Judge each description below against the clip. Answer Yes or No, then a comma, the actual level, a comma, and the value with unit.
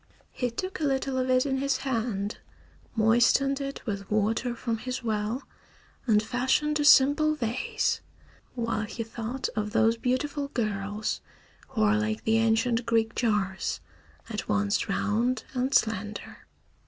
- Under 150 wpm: Yes, average, 140 wpm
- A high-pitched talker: Yes, high, 230 Hz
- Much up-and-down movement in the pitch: No, average, 3.4 semitones